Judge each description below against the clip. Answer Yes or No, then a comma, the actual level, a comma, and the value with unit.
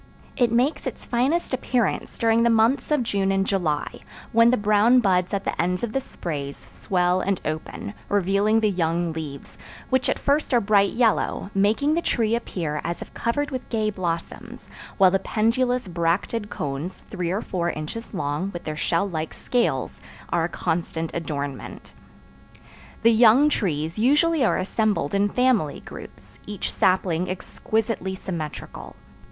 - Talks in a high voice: Yes, high, 200 Hz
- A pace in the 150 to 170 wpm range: Yes, average, 160 wpm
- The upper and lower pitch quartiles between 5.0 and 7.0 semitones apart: Yes, average, 5.3 semitones